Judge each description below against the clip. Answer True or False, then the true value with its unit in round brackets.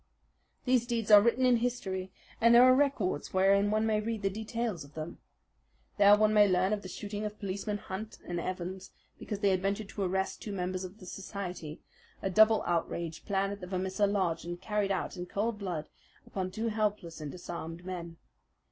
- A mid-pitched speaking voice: False (195 Hz)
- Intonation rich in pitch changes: False (2.8 semitones)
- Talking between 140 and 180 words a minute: False (195 wpm)